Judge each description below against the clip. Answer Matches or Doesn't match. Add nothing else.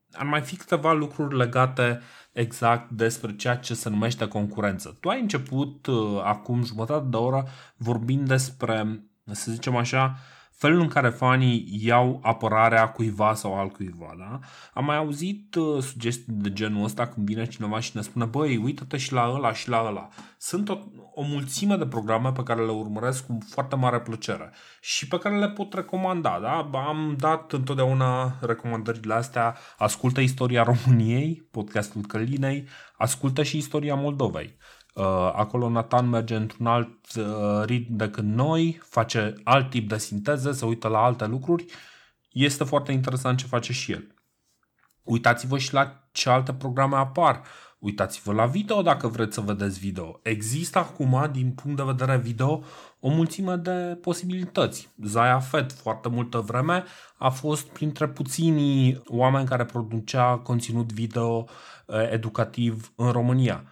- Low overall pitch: Matches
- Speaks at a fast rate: Doesn't match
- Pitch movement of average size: Matches